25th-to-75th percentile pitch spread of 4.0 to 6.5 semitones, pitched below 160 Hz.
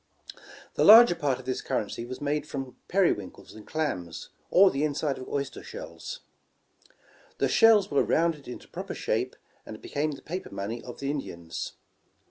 Yes: average, 5.1 semitones; medium, 140 Hz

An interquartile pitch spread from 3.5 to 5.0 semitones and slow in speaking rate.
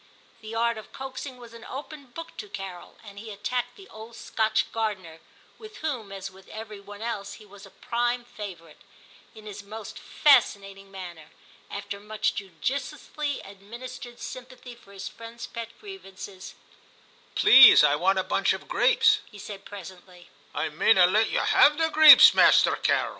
No: average, 4.1 semitones; average, 175 wpm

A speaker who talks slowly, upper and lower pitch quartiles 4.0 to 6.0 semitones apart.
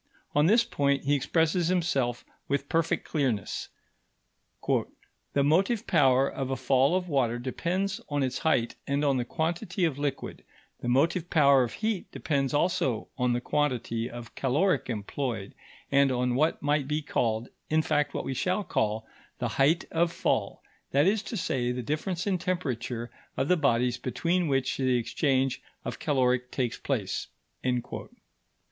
No: average, 155 wpm; average, 4.7 semitones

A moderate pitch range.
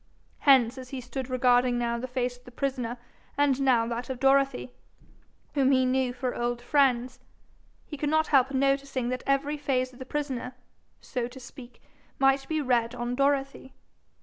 No: narrow, 1.9 semitones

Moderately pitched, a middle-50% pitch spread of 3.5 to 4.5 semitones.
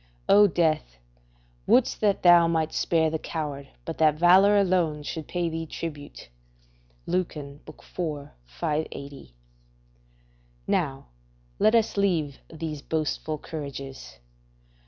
No: medium, 160 Hz; average, 3.1 semitones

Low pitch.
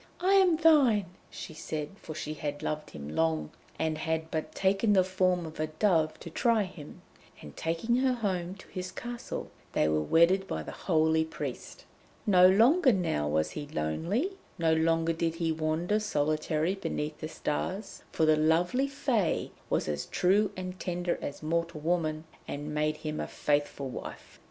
No: medium, 165 Hz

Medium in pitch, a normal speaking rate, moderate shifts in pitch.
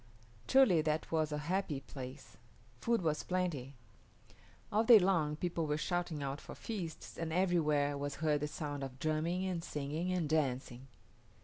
Yes: medium, 155 Hz; average, 155 wpm; average, 3.6 semitones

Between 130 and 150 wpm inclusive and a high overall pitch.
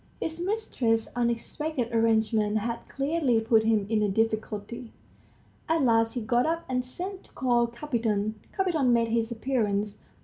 Yes: average, 145 wpm; high, 235 Hz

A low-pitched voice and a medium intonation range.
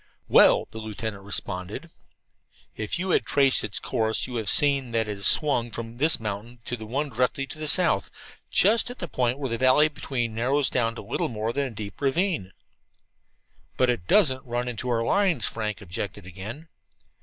Yes: low, 120 Hz; average, 4.4 semitones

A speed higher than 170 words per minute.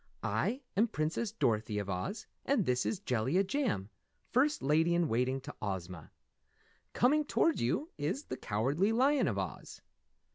No: average, 150 wpm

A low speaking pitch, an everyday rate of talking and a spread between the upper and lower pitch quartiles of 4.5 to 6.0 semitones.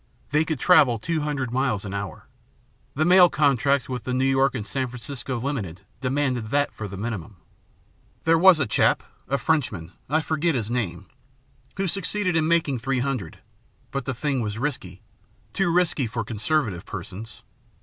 Yes: low, 130 Hz; average, 170 wpm; average, 5.3 semitones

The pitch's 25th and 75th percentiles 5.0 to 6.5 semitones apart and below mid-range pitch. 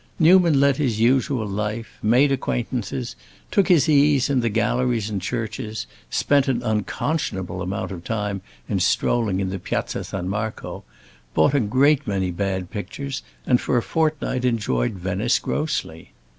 Yes: wide, 5.5 semitones; low, 115 Hz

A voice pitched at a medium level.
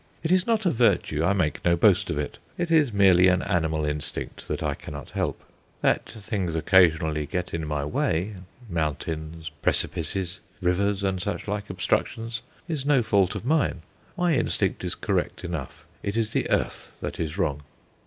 No: very low, 90 Hz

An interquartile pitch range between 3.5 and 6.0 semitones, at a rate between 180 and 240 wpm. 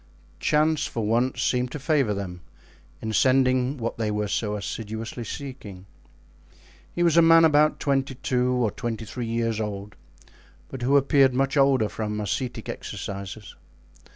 No: average, 4.2 semitones; average, 150 wpm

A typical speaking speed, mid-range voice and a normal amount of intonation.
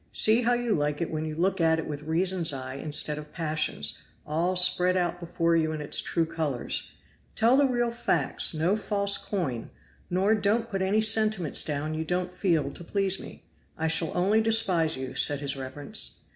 Yes: average, 190 wpm; medium, 170 Hz; average, 4.6 semitones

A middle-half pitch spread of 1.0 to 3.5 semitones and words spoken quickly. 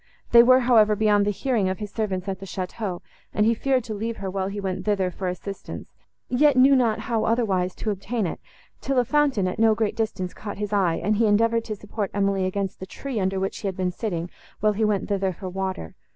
Yes: average, 3.1 semitones; fast, 235 wpm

